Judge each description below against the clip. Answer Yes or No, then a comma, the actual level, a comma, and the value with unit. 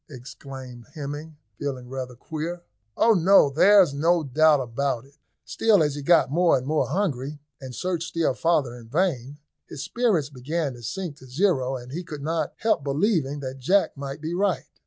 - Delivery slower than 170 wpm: No, average, 180 wpm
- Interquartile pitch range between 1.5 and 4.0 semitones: No, average, 4.4 semitones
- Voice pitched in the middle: Yes, medium, 145 Hz